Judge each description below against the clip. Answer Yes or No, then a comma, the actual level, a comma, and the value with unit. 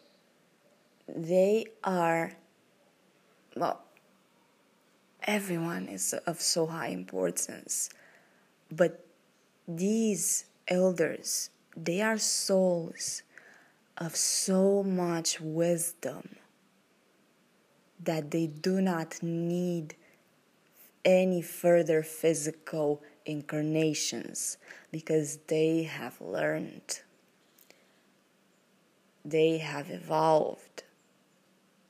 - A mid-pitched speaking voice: Yes, medium, 170 Hz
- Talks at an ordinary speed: No, slow, 65 wpm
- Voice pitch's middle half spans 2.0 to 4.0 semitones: Yes, average, 2.7 semitones